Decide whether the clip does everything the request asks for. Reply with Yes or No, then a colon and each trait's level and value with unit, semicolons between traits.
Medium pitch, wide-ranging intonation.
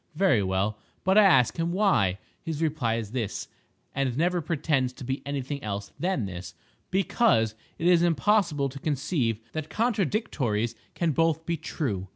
Yes: medium, 145 Hz; wide, 7.0 semitones